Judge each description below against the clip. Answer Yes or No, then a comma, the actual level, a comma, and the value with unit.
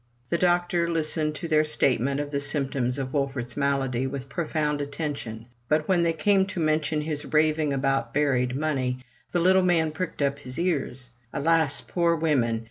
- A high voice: No, medium, 150 Hz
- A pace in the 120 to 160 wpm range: No, average, 170 wpm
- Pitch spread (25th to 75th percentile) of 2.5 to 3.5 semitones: Yes, average, 3.1 semitones